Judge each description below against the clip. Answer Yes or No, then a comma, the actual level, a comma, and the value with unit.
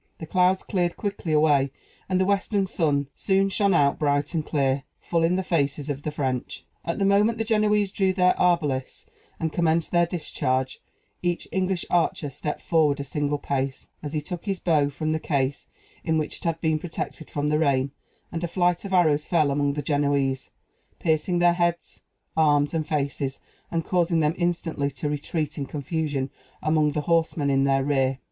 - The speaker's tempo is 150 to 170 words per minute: No, average, 185 wpm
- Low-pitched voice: No, medium, 155 Hz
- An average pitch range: Yes, average, 3.6 semitones